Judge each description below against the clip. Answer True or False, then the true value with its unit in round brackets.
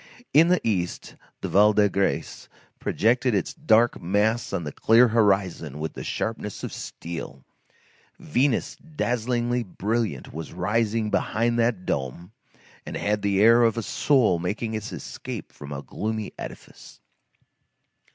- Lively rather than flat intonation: False (4.4 semitones)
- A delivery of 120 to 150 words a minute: True (140 wpm)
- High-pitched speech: False (105 Hz)